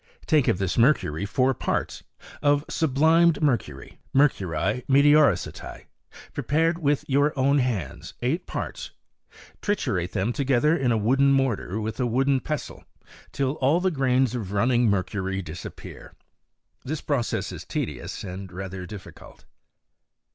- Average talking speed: No, slow, 130 wpm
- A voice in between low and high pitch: No, low, 130 Hz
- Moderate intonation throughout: No, wide, 6.2 semitones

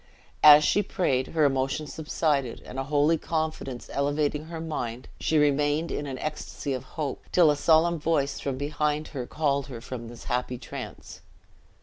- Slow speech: No, average, 165 wpm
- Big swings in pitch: No, narrow, 2.6 semitones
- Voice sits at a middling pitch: Yes, medium, 145 Hz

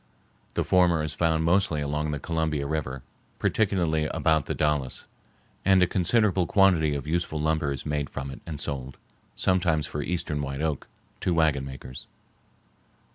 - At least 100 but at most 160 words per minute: Yes, average, 155 wpm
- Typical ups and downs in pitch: Yes, average, 3.0 semitones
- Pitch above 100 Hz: No, very low, 80 Hz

